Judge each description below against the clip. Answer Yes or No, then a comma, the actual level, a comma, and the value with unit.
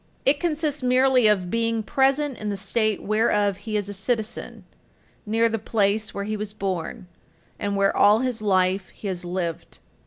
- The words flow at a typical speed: Yes, average, 175 wpm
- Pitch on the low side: No, high, 215 Hz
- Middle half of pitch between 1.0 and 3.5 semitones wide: Yes, average, 2.8 semitones